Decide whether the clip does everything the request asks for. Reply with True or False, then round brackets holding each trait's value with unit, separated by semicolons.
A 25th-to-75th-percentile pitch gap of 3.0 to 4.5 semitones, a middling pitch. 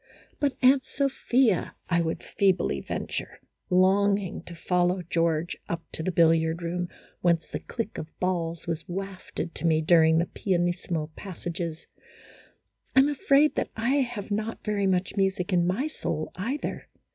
True (3.6 semitones; 180 Hz)